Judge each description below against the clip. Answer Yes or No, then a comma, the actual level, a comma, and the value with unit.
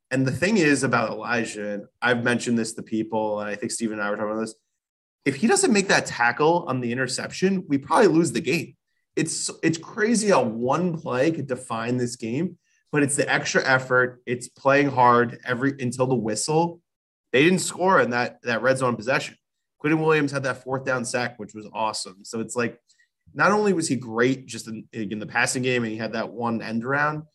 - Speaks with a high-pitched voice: No, low, 125 Hz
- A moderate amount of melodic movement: Yes, average, 5.0 semitones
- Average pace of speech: No, fast, 215 wpm